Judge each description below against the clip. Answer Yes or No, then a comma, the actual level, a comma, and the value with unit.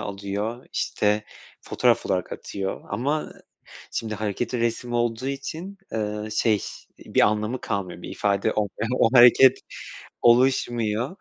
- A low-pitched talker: Yes, low, 115 Hz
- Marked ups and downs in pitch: No, average, 2.8 semitones